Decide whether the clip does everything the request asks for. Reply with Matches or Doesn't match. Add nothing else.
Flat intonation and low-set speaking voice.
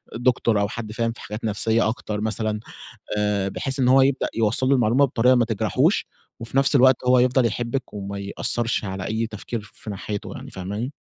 Doesn't match